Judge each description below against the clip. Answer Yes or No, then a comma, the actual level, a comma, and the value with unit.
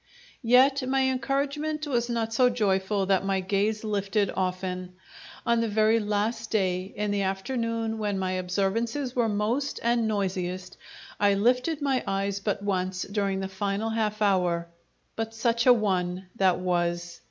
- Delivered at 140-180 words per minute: Yes, average, 155 wpm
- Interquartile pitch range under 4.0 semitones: Yes, average, 3.4 semitones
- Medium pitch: No, high, 210 Hz